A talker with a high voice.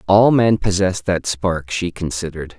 No: very low, 90 Hz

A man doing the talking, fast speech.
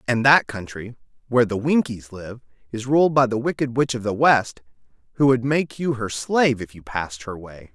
Yes: male; fast, 210 wpm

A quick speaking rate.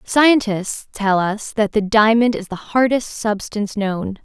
No: average, 155 wpm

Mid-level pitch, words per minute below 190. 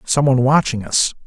No: low, 130 Hz; average, 140 wpm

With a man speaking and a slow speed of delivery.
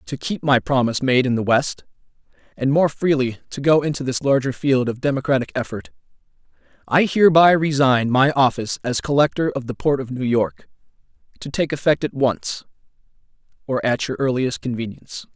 No: male; average, 170 wpm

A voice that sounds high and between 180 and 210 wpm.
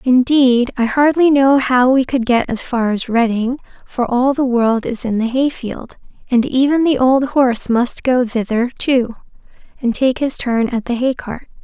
Yes: very high, 250 Hz; average, 195 wpm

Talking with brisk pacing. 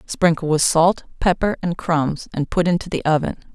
No: average, 185 wpm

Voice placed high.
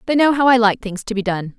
Yes: high, 225 Hz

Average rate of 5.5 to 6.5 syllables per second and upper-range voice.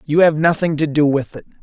No: 5.8 syllables/s; medium, 155 Hz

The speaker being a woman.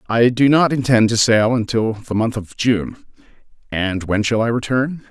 No: male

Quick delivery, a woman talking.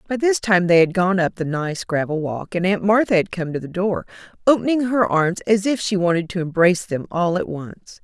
Yes: fast, 240 wpm; female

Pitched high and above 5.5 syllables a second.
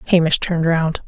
No: medium, 170 Hz; 6.2 syllables/s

